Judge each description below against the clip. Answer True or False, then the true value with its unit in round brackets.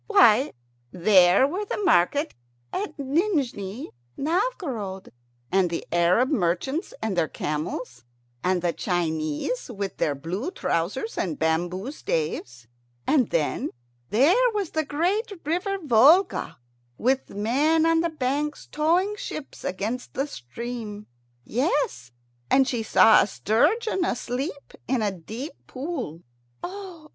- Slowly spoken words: True (125 wpm)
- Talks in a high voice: True (250 Hz)